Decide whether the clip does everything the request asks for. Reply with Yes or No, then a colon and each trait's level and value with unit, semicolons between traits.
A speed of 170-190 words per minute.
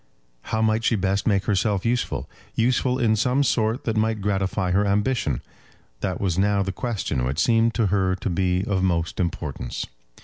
Yes: average, 175 wpm